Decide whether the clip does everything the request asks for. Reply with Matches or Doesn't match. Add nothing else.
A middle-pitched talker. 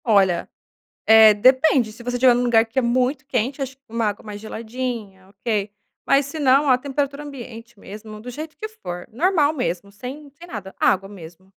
Doesn't match